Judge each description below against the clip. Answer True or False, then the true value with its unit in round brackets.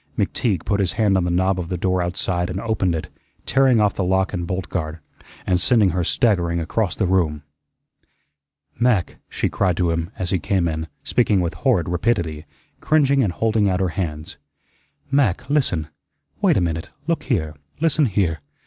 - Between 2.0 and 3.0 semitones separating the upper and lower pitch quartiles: False (3.7 semitones)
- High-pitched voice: False (95 Hz)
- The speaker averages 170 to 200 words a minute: True (180 wpm)